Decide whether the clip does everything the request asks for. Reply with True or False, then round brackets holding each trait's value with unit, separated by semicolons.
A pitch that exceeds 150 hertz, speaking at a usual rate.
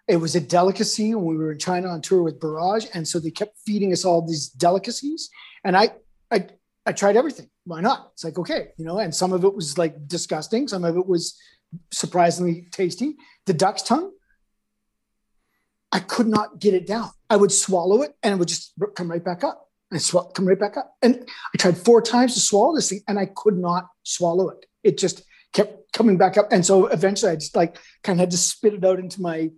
False (190 Hz; 225 wpm)